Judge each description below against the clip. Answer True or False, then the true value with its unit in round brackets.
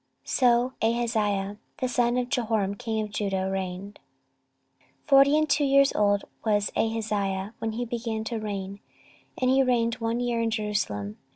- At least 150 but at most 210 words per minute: True (160 wpm)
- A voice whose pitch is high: True (225 Hz)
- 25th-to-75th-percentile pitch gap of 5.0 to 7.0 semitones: False (3.1 semitones)